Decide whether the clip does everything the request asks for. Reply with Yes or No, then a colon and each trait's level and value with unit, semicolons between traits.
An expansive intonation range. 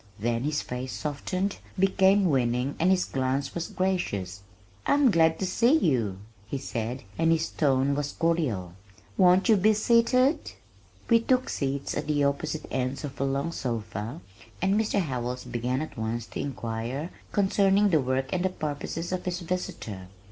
Yes: wide, 6.7 semitones